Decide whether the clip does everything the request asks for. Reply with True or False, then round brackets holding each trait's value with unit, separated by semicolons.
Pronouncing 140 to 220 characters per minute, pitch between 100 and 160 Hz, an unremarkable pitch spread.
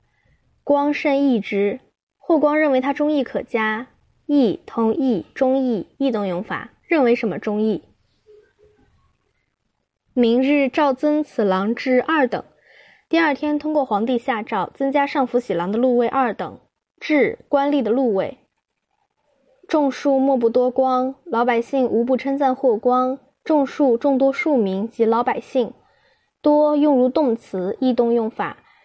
False (205 characters per minute; 265 Hz; 3.6 semitones)